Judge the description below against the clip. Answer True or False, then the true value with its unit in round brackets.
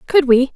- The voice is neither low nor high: False (275 Hz)